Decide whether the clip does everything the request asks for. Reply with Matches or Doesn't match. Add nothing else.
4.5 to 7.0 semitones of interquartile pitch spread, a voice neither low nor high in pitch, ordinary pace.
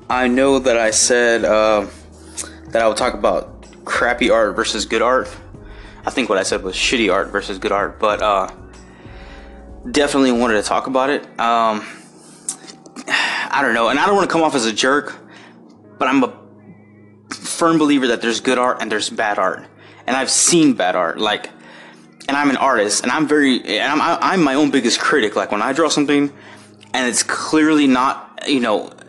Doesn't match